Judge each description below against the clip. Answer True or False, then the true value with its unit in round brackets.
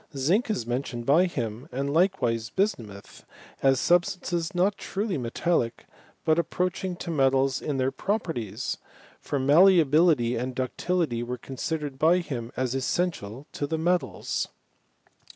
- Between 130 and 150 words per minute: True (135 wpm)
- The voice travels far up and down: True (5.9 semitones)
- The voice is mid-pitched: True (145 Hz)